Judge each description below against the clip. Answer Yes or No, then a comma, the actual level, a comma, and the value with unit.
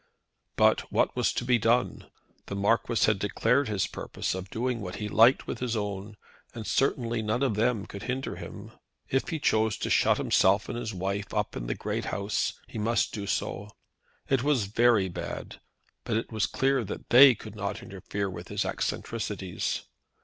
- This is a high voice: No, low, 110 Hz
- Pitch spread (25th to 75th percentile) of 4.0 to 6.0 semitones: No, average, 3.2 semitones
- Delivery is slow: No, average, 185 wpm